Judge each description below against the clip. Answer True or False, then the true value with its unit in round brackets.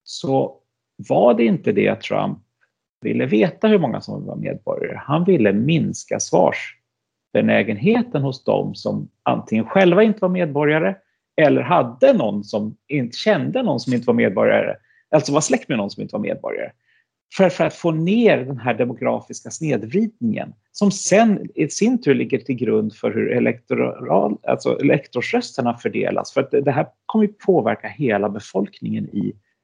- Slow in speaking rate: False (160 wpm)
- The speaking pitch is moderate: True (175 Hz)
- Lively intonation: True (8.4 semitones)